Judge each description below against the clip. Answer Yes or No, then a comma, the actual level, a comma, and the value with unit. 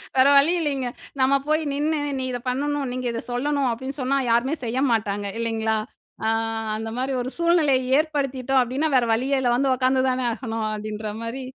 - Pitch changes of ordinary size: Yes, average, 3.1 semitones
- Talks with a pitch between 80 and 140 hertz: No, very high, 260 Hz